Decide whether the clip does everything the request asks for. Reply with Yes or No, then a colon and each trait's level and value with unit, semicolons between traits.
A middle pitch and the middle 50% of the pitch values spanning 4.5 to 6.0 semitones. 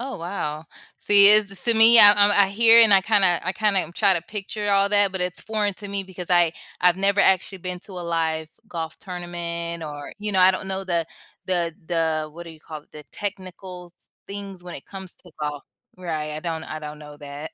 No: medium, 180 Hz; average, 3.4 semitones